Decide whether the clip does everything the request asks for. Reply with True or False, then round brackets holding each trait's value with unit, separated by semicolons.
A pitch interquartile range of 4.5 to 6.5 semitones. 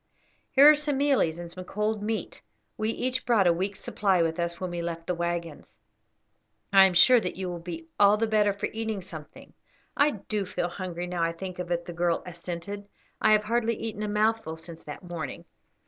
False (3.9 semitones)